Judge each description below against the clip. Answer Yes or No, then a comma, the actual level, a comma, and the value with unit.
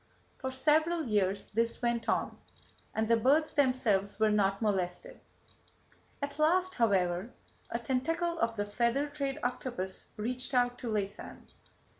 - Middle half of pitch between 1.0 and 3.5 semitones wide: No, average, 5.3 semitones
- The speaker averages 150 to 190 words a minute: No, slow, 135 wpm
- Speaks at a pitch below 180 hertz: No, high, 240 Hz